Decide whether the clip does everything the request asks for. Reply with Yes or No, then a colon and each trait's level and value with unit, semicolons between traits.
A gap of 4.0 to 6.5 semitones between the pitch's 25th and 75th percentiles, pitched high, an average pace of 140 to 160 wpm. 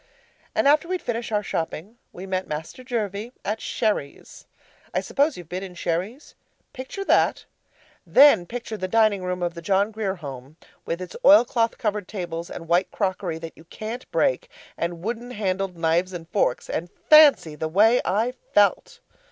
No: average, 5.2 semitones; high, 200 Hz; average, 170 wpm